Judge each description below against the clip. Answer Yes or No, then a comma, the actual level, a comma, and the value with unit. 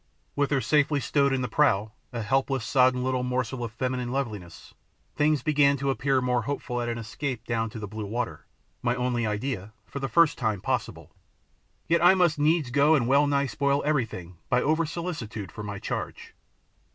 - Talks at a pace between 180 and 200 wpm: Yes, average, 185 wpm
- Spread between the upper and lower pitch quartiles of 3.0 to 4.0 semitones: Yes, average, 3.6 semitones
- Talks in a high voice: No, low, 130 Hz